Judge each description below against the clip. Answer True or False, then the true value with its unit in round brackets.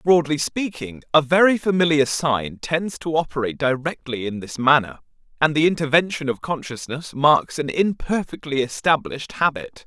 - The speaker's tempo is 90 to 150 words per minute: True (140 wpm)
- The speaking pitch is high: False (150 Hz)